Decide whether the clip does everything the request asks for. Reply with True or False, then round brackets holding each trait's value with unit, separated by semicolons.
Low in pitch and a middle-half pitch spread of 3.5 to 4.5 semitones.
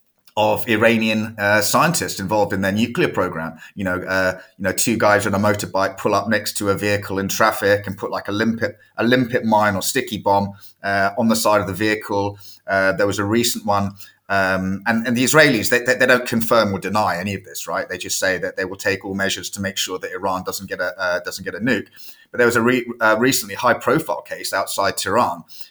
False (105 Hz; 2.6 semitones)